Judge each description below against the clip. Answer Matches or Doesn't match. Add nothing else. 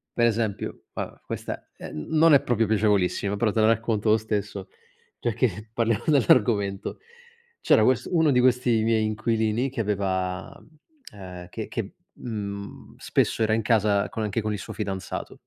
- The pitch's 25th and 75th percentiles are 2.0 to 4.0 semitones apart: Matches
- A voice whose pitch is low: Matches